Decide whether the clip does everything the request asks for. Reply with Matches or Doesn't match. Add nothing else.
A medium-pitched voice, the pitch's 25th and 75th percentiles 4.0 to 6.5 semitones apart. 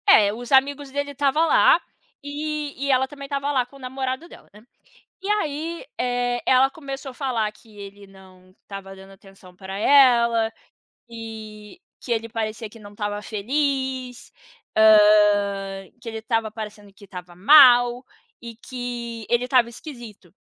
Doesn't match